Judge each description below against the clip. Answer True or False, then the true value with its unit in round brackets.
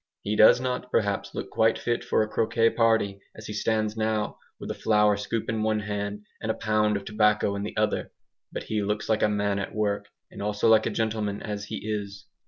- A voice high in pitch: False (105 Hz)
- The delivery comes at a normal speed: False (220 wpm)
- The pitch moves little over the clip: True (1.2 semitones)